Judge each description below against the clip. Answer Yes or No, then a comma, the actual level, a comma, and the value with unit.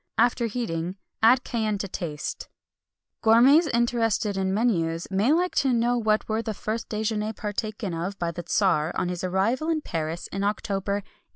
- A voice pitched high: Yes, high, 210 Hz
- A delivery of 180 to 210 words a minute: No, average, 170 wpm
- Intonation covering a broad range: No, average, 3.8 semitones